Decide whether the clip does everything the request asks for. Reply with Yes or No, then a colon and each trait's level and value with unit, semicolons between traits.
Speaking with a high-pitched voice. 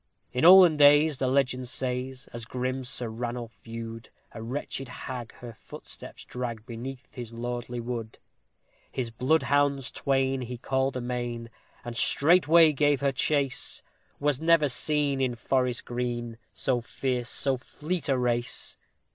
No: low, 125 Hz